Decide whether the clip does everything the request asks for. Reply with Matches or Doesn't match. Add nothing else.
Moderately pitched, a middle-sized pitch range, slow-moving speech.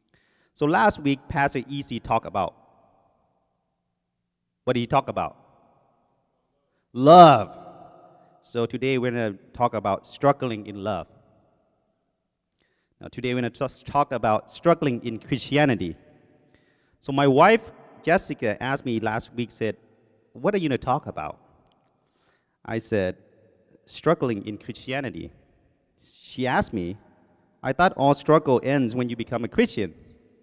Doesn't match